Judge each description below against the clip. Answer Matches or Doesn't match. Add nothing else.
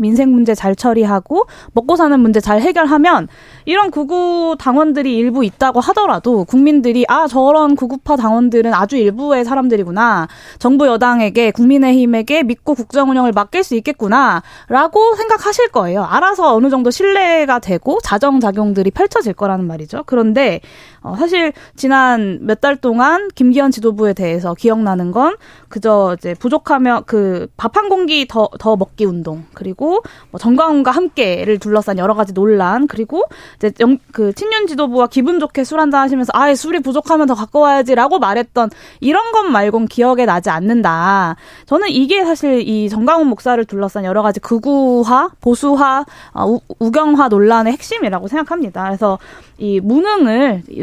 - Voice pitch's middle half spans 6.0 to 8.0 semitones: Doesn't match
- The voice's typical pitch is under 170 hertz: Doesn't match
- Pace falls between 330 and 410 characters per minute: Matches